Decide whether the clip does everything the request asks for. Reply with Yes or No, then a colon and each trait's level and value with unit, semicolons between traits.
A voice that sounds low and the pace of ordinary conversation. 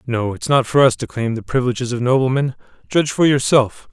No: low, 125 Hz; fast, 215 wpm